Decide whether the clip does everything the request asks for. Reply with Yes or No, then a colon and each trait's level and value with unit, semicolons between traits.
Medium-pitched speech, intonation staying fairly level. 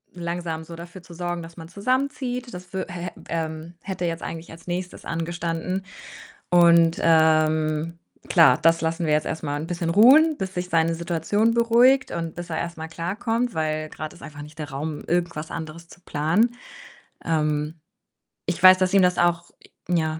Yes: medium, 170 Hz; narrow, 2.2 semitones